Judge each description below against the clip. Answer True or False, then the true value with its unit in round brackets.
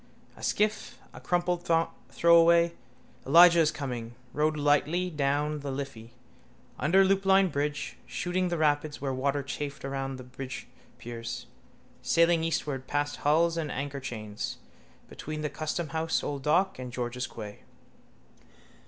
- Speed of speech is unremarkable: False (125 wpm)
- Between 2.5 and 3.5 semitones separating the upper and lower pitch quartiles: False (3.9 semitones)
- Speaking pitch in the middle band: True (145 Hz)